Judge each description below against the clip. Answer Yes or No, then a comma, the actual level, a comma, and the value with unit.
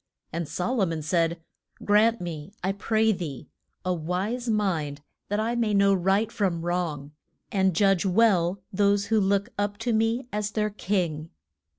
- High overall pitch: Yes, high, 195 Hz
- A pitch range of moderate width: Yes, average, 3.7 semitones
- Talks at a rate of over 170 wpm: No, average, 165 wpm